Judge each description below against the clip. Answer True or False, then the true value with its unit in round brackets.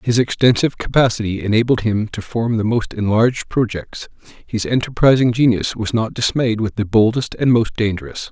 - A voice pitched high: False (115 Hz)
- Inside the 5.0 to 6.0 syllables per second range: True (5.2 syllables/s)